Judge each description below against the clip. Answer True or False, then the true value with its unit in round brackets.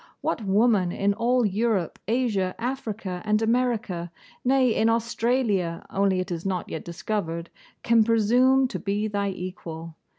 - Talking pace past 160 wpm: False (140 wpm)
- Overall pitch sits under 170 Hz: False (210 Hz)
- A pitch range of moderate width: True (4.1 semitones)